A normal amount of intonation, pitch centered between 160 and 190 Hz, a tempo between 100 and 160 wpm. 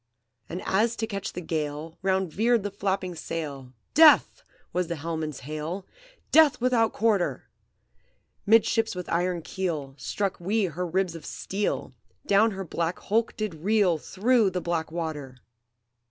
Yes: average, 4.4 semitones; medium, 185 Hz; average, 145 wpm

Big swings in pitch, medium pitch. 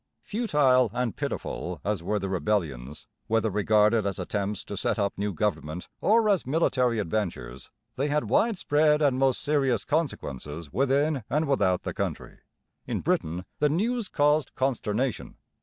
No: wide, 7.0 semitones; low, 115 Hz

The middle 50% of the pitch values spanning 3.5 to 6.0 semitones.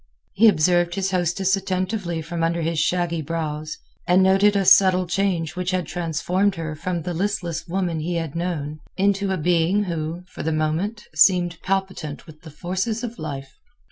No: average, 2.9 semitones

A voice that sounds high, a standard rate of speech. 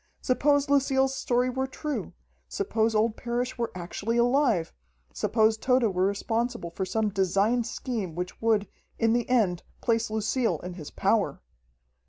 Yes: high, 230 Hz; average, 145 wpm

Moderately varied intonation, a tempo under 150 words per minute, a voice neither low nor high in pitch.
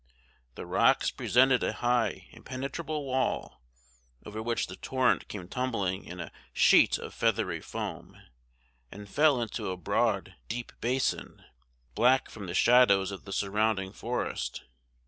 No: average, 4.8 semitones; slow, 135 wpm; low, 115 Hz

